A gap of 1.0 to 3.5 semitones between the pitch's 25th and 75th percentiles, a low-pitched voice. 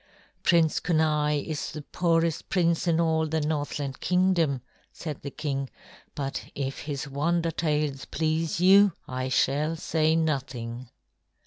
No: average, 2.8 semitones; medium, 155 Hz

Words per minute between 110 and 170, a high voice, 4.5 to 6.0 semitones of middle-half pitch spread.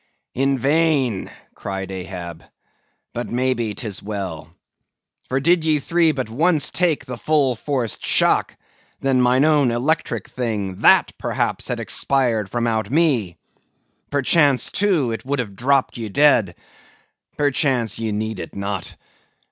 No: slow, 135 wpm; low, 125 Hz; average, 5.1 semitones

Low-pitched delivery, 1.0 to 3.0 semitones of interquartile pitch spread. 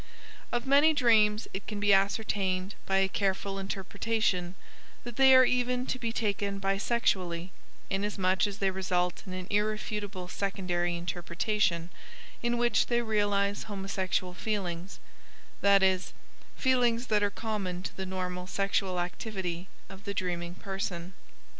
No: high, 195 Hz; average, 2.7 semitones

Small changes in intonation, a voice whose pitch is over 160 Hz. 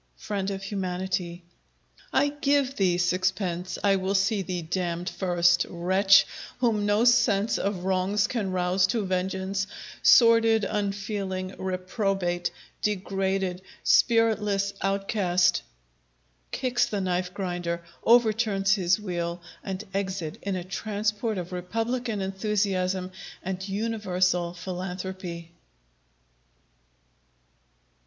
Yes: narrow, 2.2 semitones; high, 190 Hz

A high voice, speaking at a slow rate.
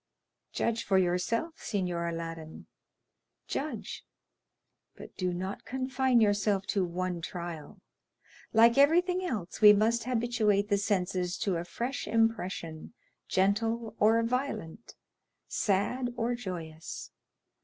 Yes: high, 205 Hz; slow, 105 wpm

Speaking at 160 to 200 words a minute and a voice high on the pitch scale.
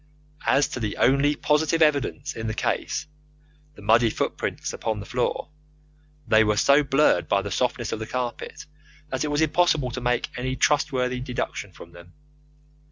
No: average, 165 wpm; low, 125 Hz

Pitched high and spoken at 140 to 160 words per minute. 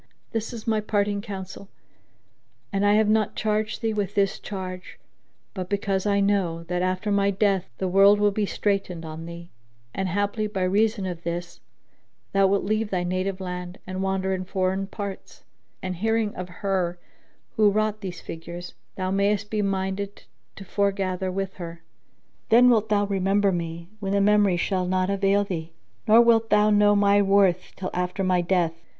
No: high, 195 Hz; average, 175 wpm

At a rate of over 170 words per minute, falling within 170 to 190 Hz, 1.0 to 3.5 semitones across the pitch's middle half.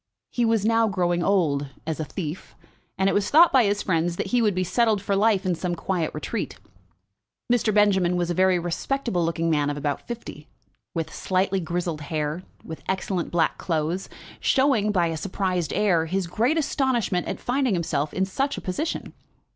No: average, 185 wpm; medium, 185 Hz; average, 4.1 semitones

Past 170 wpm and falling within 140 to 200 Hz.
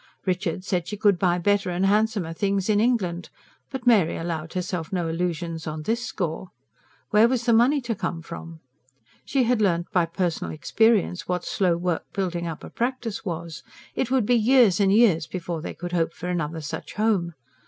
Yes: average, 185 wpm; medium, 185 Hz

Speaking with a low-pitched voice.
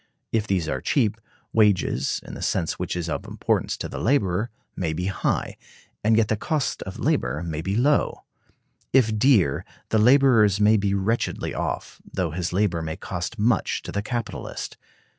Yes: low, 105 Hz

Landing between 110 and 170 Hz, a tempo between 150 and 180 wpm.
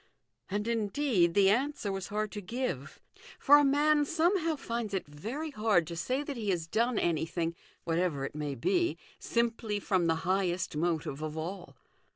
No: high, 200 Hz; average, 170 wpm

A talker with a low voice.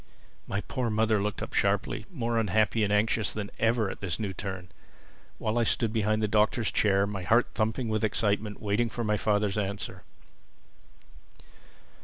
Yes: low, 105 Hz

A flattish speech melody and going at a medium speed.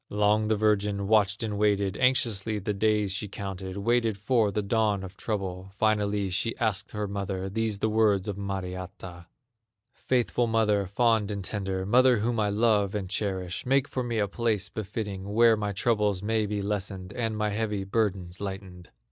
Yes: narrow, 2.1 semitones; average, 175 wpm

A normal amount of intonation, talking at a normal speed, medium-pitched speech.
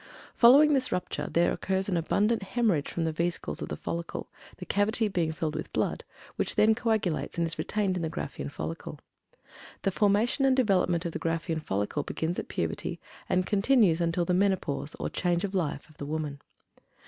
Yes: average, 4.2 semitones; average, 185 wpm; medium, 180 Hz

